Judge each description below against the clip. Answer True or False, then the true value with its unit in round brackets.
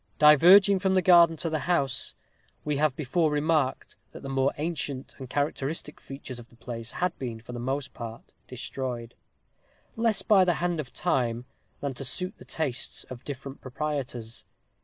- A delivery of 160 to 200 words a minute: True (170 wpm)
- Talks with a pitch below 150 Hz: True (140 Hz)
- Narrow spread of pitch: False (4.5 semitones)